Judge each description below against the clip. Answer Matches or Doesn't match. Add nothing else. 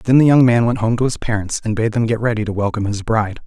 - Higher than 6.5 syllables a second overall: Matches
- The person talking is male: Matches